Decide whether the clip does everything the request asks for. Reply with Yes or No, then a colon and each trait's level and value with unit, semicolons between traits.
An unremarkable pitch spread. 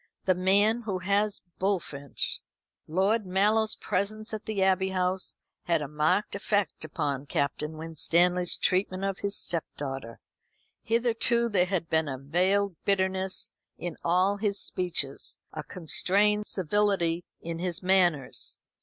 Yes: average, 3.3 semitones